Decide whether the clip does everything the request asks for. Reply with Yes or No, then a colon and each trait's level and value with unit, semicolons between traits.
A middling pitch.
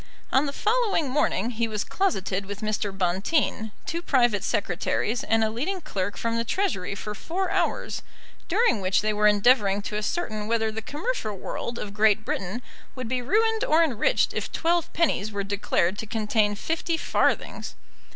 No: high, 225 Hz